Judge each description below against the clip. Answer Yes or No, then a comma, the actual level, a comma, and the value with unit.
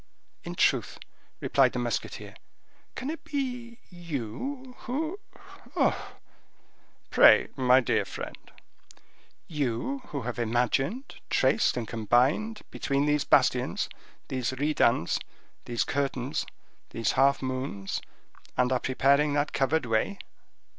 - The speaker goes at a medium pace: No, slow, 100 wpm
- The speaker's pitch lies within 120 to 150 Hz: Yes, medium, 140 Hz